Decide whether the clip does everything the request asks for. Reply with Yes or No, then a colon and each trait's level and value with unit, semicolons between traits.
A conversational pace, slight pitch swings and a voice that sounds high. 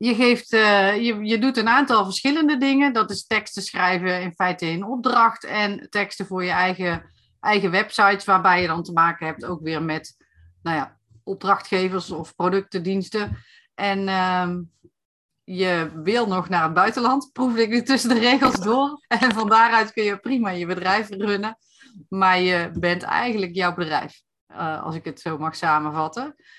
No: average, 175 wpm; average, 4.4 semitones; high, 195 Hz